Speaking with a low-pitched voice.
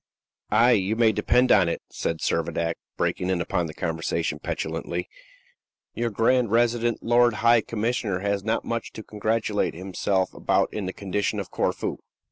Yes: low, 105 Hz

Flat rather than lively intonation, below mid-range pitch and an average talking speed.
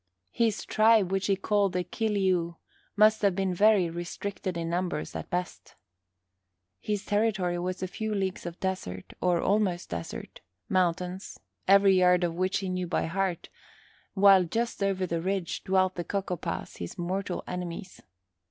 No: narrow, 2.0 semitones; medium, 185 Hz; average, 160 wpm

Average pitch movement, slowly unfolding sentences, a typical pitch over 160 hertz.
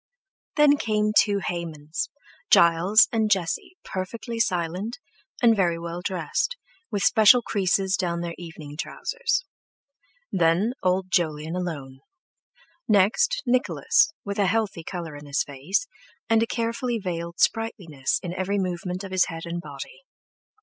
Yes: average, 4.8 semitones; slow, 130 wpm; medium, 185 Hz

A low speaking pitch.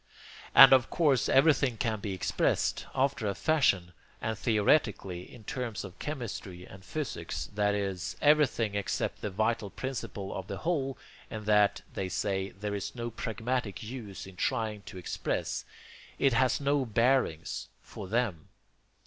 Yes: low, 110 Hz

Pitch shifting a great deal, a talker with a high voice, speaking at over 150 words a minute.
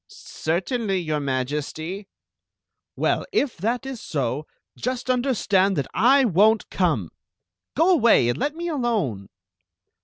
No: wide, 8.5 semitones; high, 205 Hz; average, 140 wpm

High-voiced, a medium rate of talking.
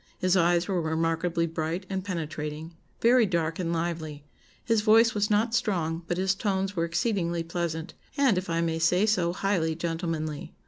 No: medium, 170 Hz; average, 170 wpm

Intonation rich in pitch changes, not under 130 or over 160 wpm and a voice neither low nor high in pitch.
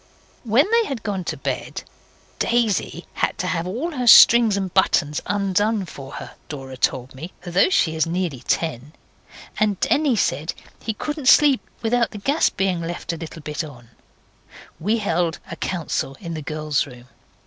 No: wide, 6.3 semitones; average, 170 wpm; medium, 180 Hz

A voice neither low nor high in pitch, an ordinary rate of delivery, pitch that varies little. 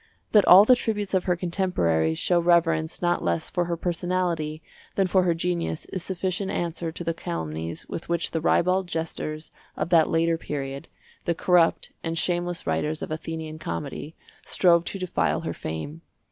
Yes: medium, 170 Hz; average, 170 wpm; narrow, 2.3 semitones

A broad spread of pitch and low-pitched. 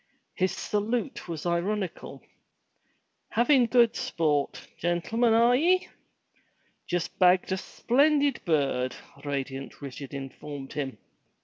No: wide, 8.6 semitones; medium, 180 Hz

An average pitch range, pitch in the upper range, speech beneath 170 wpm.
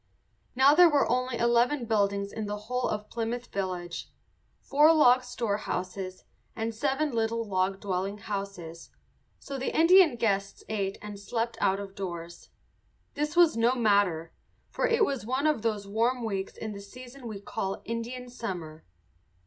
Yes: average, 4.1 semitones; high, 225 Hz; average, 155 wpm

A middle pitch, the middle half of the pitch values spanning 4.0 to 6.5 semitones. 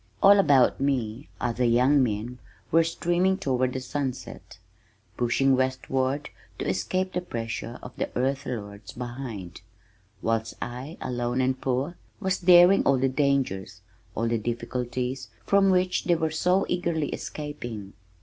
No: low, 130 Hz; average, 4.8 semitones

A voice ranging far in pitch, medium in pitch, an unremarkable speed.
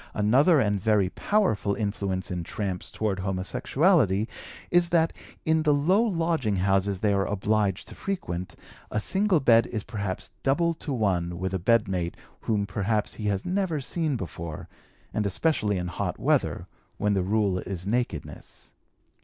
No: wide, 7.2 semitones; low, 105 Hz; average, 155 wpm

